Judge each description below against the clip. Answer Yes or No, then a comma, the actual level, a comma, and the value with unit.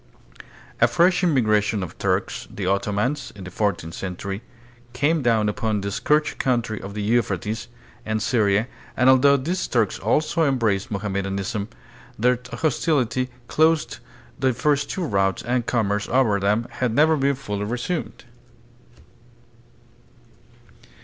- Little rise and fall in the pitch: No, average, 5.0 semitones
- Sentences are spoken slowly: Yes, slow, 130 wpm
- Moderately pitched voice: No, low, 115 Hz